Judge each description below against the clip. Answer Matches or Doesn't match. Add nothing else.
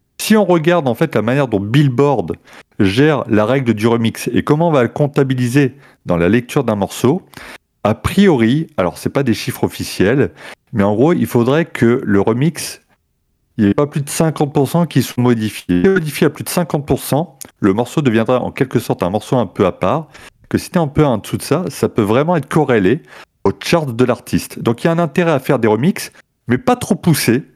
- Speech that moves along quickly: Matches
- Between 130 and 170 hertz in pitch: Matches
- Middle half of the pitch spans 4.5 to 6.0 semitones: Matches